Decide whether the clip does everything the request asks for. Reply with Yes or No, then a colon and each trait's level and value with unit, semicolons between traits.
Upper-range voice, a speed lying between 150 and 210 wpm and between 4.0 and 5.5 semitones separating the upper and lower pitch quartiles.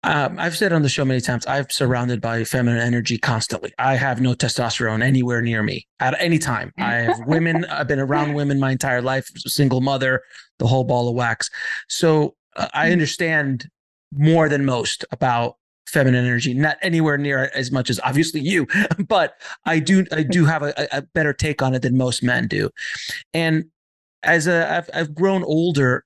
No: medium, 140 Hz; average, 190 wpm; average, 4.3 semitones